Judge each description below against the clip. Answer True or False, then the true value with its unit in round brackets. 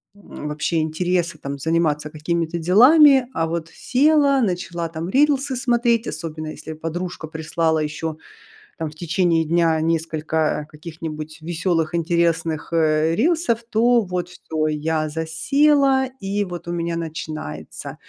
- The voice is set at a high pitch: False (165 Hz)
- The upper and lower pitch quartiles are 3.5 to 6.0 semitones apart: True (3.9 semitones)